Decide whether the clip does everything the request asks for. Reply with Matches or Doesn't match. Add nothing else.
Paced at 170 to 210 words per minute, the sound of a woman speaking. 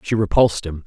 Doesn't match